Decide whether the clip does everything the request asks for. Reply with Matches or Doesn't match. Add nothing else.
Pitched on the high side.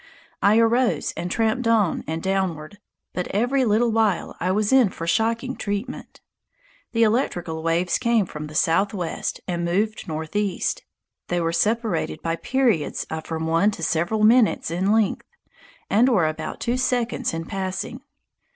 Matches